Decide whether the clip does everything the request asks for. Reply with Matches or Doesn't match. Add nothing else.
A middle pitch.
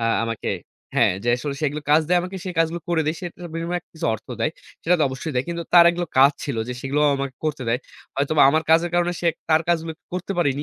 Matches